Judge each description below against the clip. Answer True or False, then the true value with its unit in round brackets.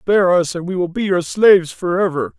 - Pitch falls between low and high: True (170 Hz)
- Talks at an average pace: False (225 wpm)